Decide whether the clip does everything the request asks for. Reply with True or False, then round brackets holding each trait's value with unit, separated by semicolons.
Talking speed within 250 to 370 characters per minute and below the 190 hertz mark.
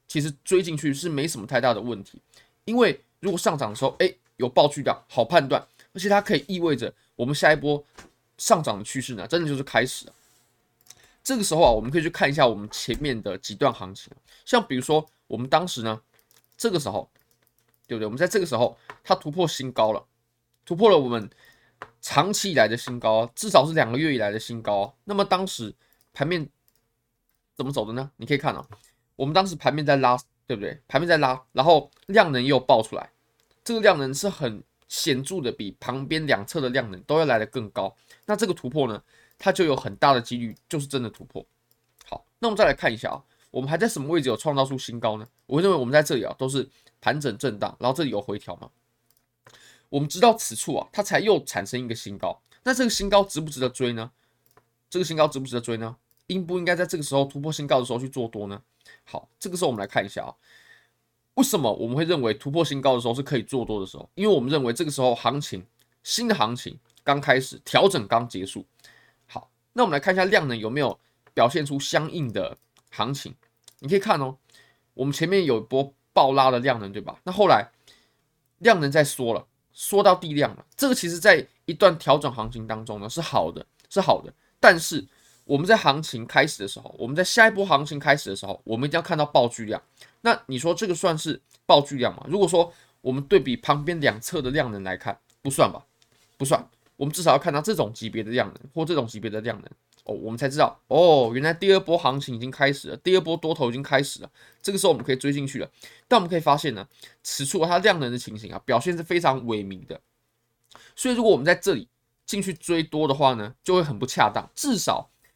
True (325 characters per minute; 135 Hz)